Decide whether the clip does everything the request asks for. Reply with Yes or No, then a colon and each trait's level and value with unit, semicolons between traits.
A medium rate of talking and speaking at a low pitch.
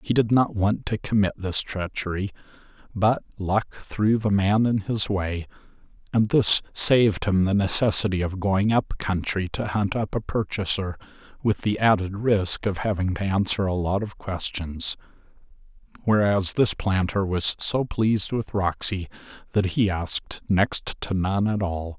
Yes: average, 160 wpm; low, 100 Hz